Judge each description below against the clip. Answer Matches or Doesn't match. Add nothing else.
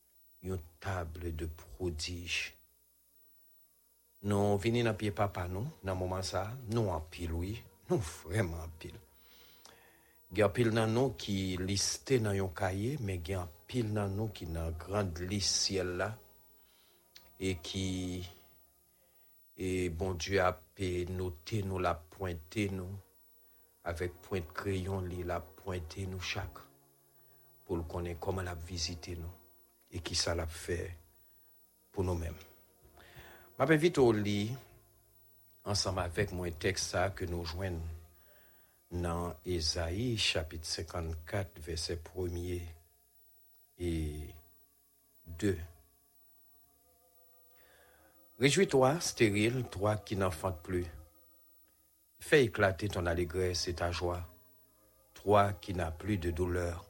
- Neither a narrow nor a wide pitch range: Matches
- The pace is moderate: Doesn't match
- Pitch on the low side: Matches